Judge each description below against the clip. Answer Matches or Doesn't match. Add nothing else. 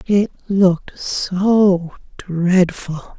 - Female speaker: Matches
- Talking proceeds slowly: Matches